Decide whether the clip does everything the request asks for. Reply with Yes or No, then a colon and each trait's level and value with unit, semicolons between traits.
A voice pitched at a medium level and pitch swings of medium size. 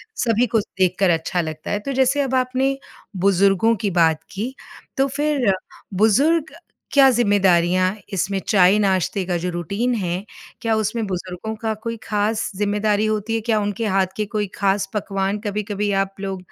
No: high, 205 Hz; average, 3.0 semitones